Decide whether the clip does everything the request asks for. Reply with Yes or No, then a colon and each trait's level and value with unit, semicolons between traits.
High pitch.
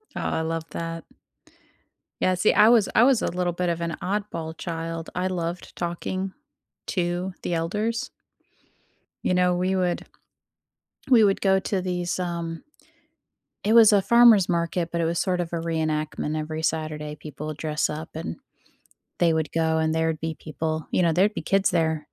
No: medium, 170 Hz